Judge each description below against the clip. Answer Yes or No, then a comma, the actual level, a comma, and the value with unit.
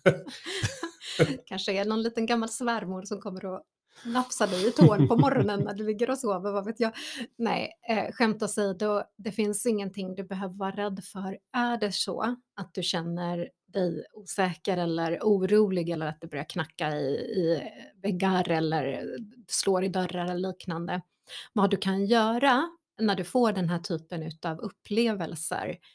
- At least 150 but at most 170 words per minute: Yes, average, 165 wpm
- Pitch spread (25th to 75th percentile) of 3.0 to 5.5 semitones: Yes, average, 3.7 semitones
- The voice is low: No, high, 200 Hz